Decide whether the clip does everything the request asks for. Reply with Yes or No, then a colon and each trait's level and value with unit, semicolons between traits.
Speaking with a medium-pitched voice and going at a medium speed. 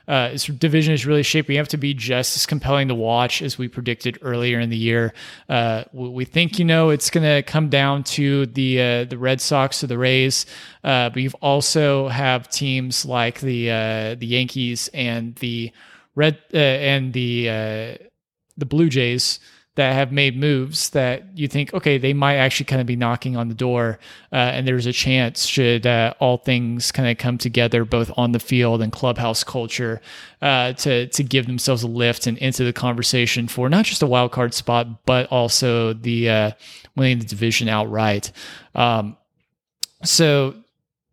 No: low, 125 Hz; average, 185 wpm